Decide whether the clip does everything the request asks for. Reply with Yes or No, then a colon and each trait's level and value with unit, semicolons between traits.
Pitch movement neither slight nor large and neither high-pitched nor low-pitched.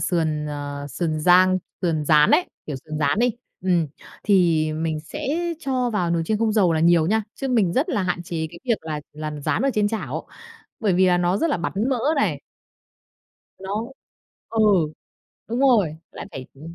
No: wide, 5.7 semitones; medium, 175 Hz